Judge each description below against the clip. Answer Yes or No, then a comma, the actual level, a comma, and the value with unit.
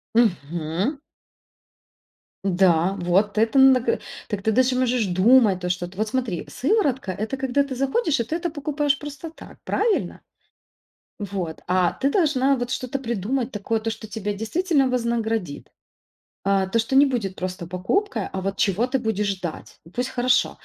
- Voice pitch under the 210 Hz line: No, high, 230 Hz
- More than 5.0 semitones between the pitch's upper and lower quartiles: Yes, wide, 5.6 semitones